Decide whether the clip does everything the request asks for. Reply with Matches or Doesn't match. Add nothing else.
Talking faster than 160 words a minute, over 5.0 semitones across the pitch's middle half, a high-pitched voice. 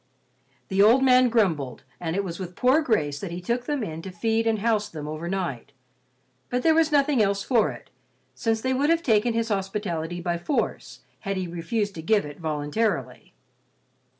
Matches